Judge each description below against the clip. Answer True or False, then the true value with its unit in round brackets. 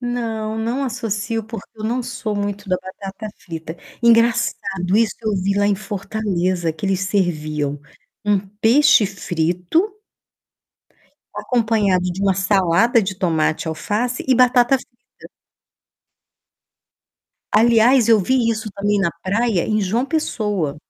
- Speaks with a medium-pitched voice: False (210 Hz)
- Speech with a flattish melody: False (3.6 semitones)